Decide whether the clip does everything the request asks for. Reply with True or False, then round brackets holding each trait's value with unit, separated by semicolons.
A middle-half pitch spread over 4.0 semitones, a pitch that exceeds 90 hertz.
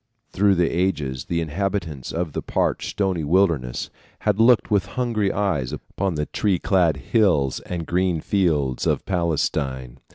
False (4.9 semitones; 85 Hz)